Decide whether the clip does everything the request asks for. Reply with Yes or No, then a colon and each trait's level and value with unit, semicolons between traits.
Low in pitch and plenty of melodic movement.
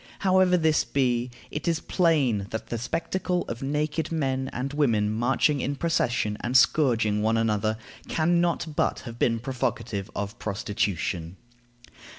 Yes: low, 125 Hz; wide, 6.0 semitones